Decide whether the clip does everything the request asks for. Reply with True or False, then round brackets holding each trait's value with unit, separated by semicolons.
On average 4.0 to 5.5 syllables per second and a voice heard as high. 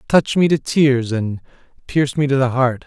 False (5.3 syllables/s; 135 Hz)